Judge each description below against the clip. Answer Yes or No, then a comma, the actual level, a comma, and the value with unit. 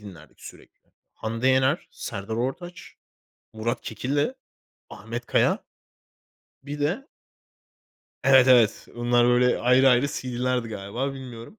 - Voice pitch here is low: Yes, low, 125 Hz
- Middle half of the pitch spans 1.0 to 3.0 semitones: Yes, narrow, 2.6 semitones